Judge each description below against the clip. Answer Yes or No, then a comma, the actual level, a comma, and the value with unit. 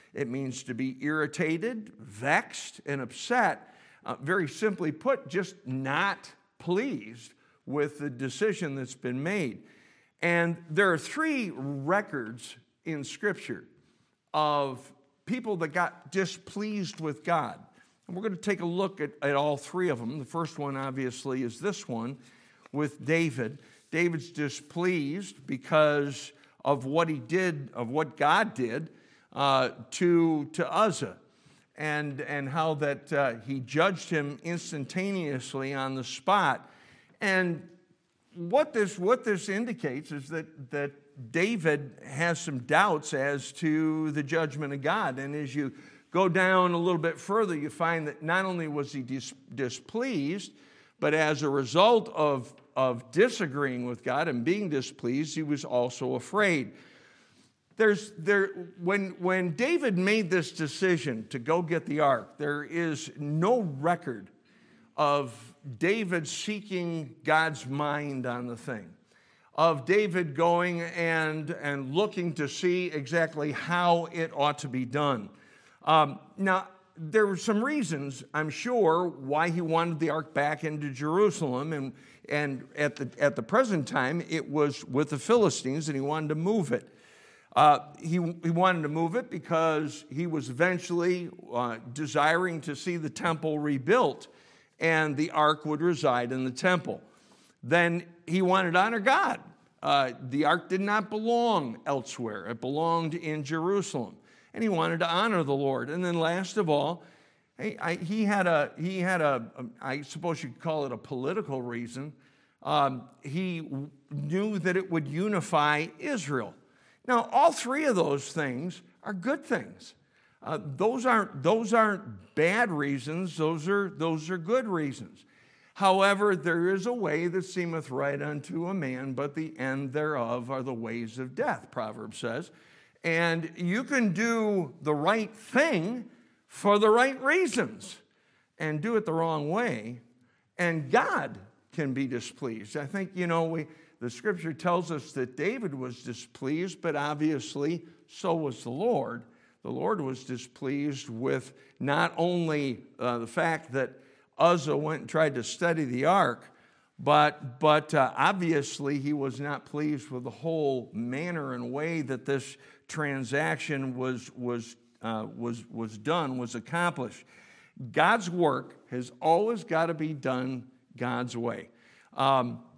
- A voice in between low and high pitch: Yes, medium, 155 Hz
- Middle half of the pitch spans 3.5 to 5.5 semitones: Yes, average, 4.5 semitones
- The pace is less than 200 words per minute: Yes, average, 150 wpm